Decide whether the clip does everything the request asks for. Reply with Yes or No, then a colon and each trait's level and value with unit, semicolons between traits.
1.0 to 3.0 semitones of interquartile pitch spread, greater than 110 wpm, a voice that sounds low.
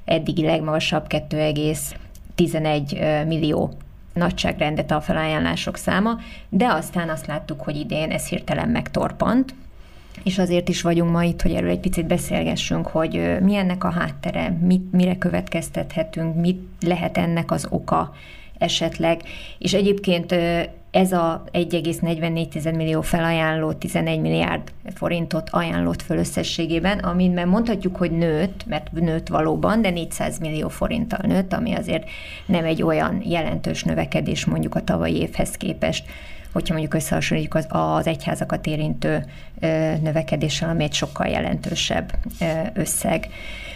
No: narrow, 2.5 semitones; average, 125 wpm; medium, 165 Hz